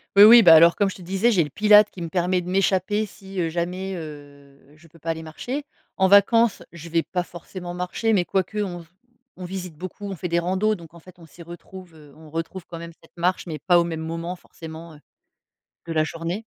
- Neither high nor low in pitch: Yes, medium, 175 Hz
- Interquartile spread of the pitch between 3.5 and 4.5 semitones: No, average, 2.7 semitones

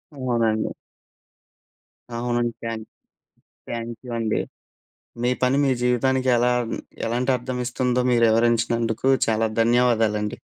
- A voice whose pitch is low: Yes, low, 120 Hz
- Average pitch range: No, narrow, 1.5 semitones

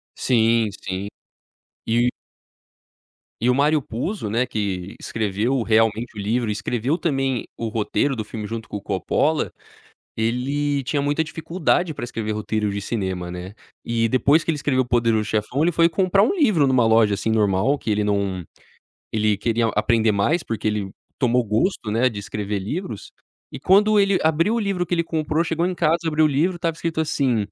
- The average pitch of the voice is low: Yes, low, 120 Hz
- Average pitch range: No, wide, 6.7 semitones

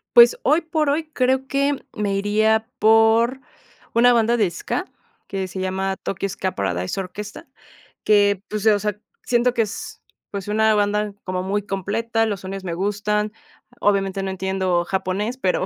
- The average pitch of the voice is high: Yes, high, 205 Hz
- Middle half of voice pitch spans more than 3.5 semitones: No, average, 3.0 semitones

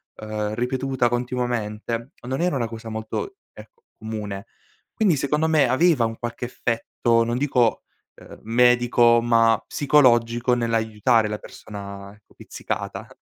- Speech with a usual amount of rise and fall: No, narrow, 2.2 semitones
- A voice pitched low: Yes, low, 120 Hz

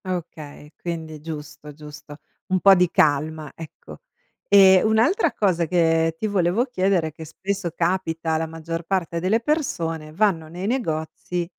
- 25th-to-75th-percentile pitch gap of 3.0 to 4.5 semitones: Yes, average, 3.3 semitones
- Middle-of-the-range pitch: Yes, medium, 170 Hz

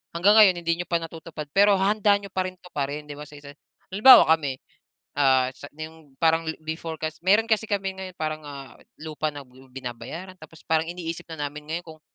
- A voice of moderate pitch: Yes, medium, 160 Hz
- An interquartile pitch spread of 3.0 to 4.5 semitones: Yes, average, 4.1 semitones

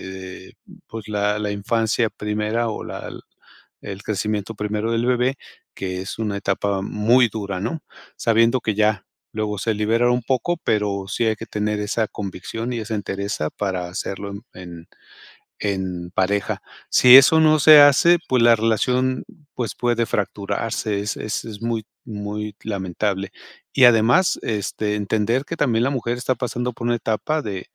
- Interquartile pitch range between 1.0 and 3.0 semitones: Yes, average, 2.7 semitones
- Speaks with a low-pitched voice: Yes, low, 110 Hz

